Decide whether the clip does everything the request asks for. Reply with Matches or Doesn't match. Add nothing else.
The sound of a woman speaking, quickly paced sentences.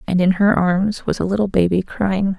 Matches